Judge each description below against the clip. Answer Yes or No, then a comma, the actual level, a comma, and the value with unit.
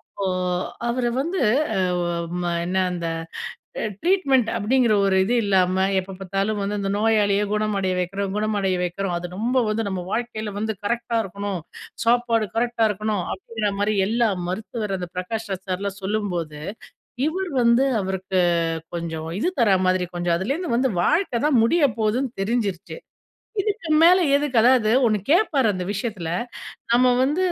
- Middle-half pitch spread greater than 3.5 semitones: Yes, average, 4.0 semitones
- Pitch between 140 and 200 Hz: No, high, 215 Hz